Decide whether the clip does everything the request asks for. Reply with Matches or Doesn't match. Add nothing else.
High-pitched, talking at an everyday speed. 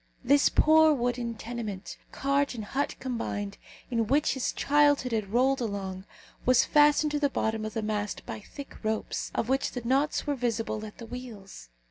Matches